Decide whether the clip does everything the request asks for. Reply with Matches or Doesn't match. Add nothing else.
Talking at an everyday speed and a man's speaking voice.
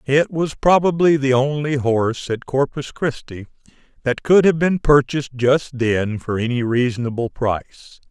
Matches